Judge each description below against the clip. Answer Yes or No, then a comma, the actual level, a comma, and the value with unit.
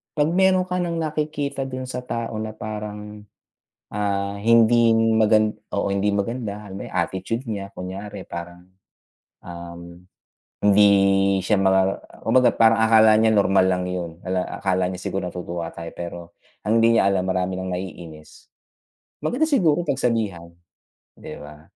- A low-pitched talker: Yes, low, 105 Hz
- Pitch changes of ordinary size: Yes, average, 3.9 semitones